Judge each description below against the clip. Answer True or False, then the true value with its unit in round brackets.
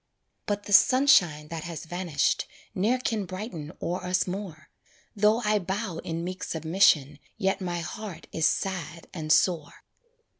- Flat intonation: False (3.9 semitones)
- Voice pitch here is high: False (180 Hz)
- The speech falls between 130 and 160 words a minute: True (145 wpm)